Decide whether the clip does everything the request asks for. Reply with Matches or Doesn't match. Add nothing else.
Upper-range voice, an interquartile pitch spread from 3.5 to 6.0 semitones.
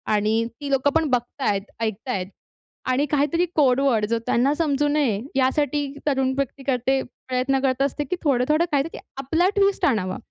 Doesn't match